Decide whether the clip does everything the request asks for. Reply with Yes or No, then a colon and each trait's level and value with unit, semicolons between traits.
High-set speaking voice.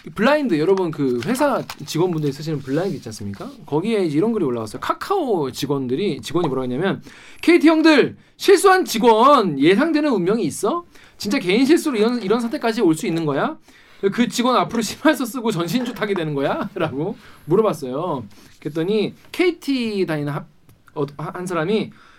Yes: high, 205 Hz